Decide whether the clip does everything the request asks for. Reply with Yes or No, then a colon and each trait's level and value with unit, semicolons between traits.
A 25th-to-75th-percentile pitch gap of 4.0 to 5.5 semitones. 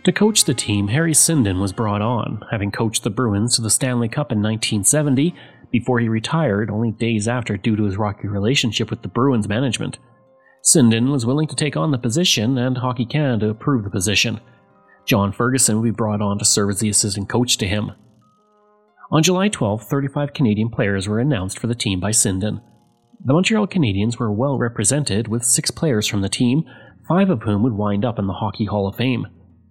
Yes: average, 4.5 semitones